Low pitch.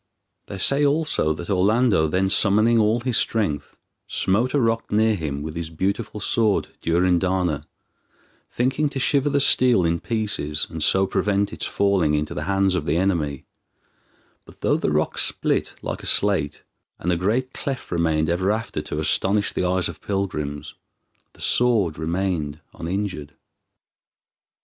Yes: very low, 95 Hz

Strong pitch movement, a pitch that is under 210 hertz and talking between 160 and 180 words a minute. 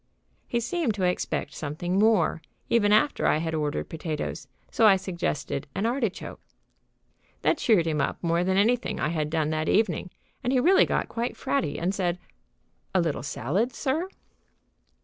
Yes: wide, 6.4 semitones; medium, 185 Hz; average, 165 wpm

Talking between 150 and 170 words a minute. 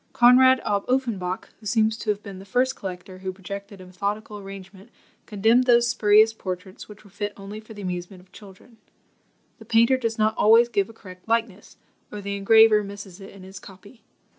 No: average, 190 wpm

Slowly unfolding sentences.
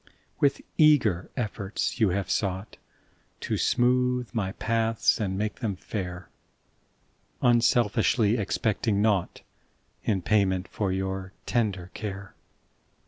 Yes: slow, 125 wpm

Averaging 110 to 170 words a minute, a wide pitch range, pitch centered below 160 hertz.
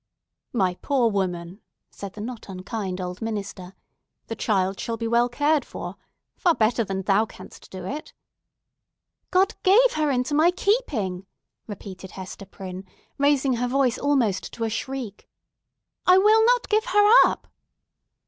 No: average, 150 wpm; wide, 7.2 semitones; high, 230 Hz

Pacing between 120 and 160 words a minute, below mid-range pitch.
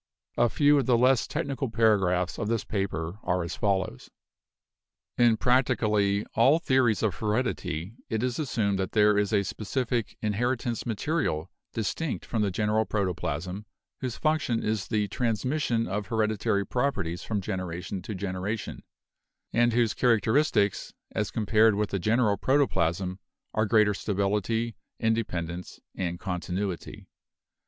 Yes: slow, 135 wpm; low, 105 Hz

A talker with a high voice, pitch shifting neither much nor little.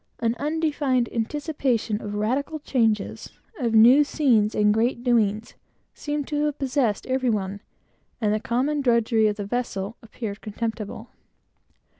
Yes: high, 235 Hz; average, 4.3 semitones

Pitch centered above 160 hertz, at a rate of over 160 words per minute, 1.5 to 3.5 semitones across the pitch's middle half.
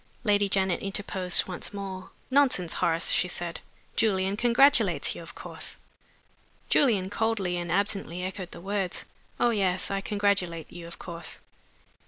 No: high, 190 Hz; average, 140 wpm; narrow, 2.5 semitones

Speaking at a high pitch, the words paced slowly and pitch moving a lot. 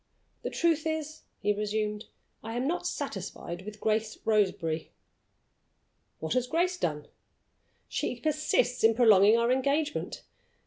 Yes: high, 225 Hz; slow, 125 wpm; wide, 6.1 semitones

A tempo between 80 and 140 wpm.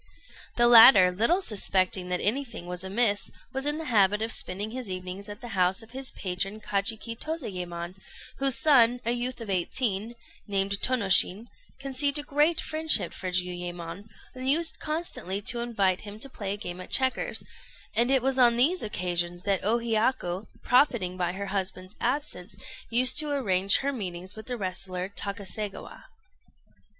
No: average, 160 wpm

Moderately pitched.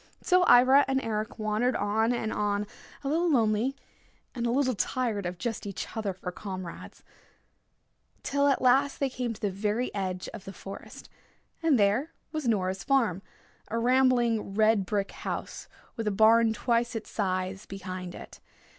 No: high, 220 Hz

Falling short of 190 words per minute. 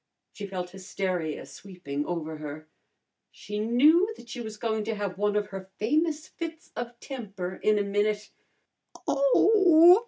Yes: average, 150 wpm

